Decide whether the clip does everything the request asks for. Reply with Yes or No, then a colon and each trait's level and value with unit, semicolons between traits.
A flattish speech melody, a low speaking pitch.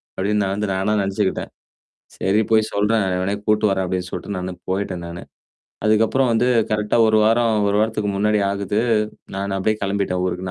Yes: narrow, 2.0 semitones; low, 100 Hz